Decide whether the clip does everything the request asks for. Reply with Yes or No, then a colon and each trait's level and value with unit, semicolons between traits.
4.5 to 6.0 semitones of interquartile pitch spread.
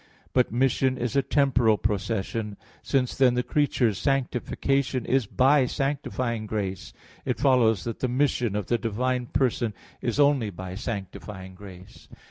No: average, 4.0 semitones